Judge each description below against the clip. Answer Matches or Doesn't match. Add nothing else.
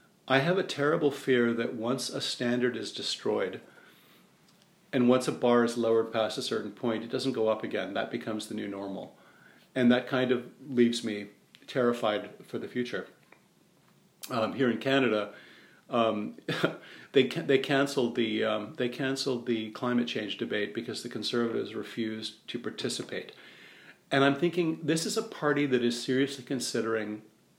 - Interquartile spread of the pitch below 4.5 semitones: Matches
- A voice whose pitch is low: Matches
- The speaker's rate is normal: Matches